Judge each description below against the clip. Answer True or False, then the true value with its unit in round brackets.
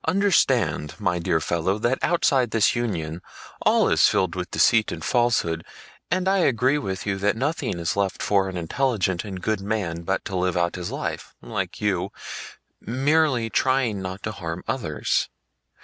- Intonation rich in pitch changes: True (5.9 semitones)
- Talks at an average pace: True (165 wpm)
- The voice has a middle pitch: False (100 Hz)